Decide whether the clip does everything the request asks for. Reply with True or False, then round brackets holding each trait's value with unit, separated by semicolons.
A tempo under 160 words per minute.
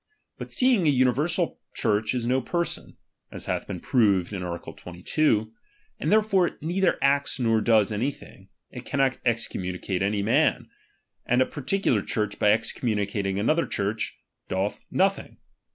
True (150 wpm)